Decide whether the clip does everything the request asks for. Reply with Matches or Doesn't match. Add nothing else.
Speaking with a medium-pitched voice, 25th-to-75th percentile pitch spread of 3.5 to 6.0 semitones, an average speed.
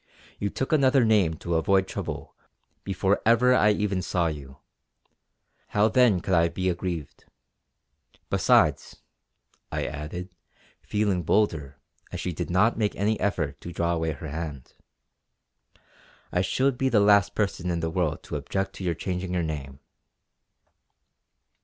Doesn't match